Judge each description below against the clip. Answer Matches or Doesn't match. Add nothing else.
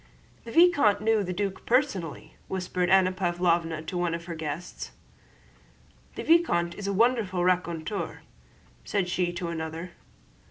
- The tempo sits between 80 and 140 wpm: Matches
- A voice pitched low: Doesn't match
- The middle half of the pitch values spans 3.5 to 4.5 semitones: Doesn't match